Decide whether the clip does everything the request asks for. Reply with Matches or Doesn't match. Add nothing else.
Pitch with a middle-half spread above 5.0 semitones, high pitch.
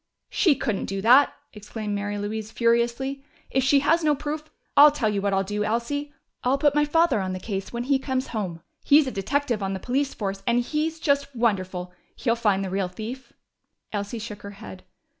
Matches